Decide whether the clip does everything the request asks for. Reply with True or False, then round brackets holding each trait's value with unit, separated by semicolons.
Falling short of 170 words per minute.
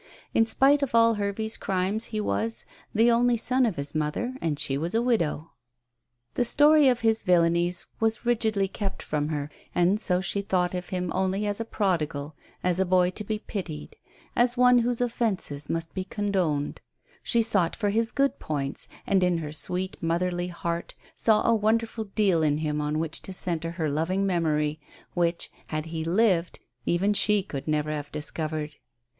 False (180 wpm)